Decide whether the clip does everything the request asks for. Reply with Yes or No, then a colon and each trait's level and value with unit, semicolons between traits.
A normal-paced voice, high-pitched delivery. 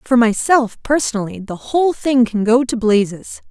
Yes: average, 170 wpm; high, 235 Hz